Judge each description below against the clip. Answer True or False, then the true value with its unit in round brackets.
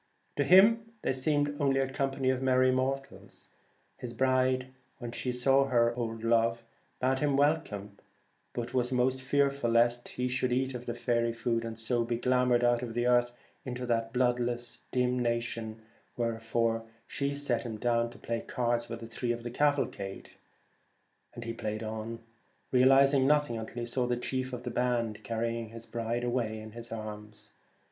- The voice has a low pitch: True (120 Hz)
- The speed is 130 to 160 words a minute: False (170 wpm)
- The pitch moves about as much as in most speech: False (2.0 semitones)